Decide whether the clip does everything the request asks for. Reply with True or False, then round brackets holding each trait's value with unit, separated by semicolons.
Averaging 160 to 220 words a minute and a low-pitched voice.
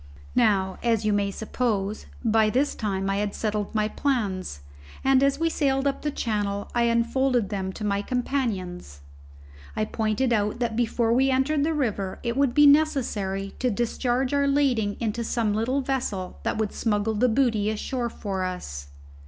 False (170 wpm; 225 Hz)